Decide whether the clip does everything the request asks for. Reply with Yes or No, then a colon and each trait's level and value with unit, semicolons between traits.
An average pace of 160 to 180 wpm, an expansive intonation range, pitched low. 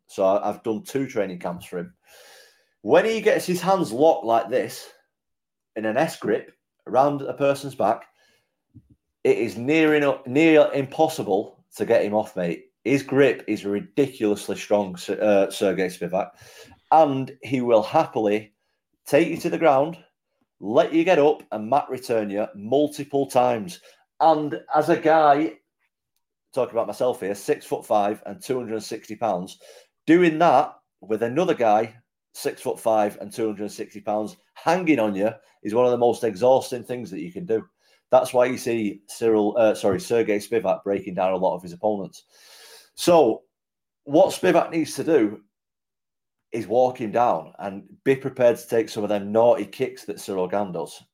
Yes: average, 170 wpm; wide, 5.7 semitones; low, 125 Hz